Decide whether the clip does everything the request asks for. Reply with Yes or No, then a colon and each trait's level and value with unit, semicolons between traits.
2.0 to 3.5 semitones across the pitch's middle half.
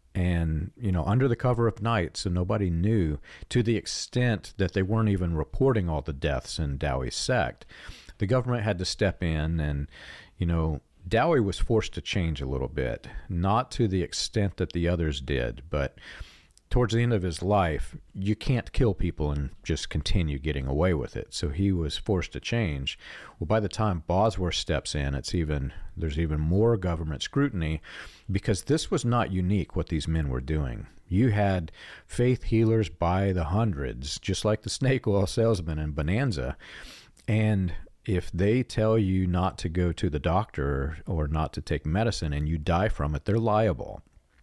No: wide, 5.6 semitones